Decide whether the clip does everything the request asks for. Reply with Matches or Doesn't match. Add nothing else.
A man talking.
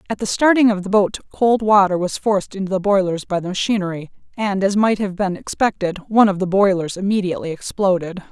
Doesn't match